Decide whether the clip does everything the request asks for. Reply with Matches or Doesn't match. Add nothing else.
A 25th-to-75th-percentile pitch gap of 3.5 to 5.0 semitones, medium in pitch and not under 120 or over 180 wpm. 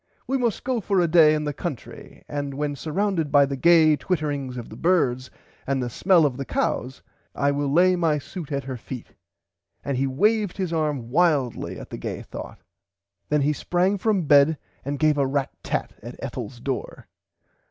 Doesn't match